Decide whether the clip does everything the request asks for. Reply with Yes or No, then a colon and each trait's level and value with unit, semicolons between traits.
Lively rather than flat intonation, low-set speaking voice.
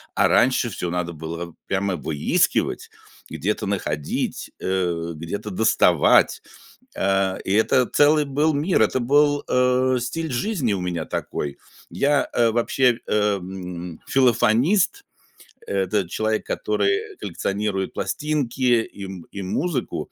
Yes: wide, 5.8 semitones; low, 105 Hz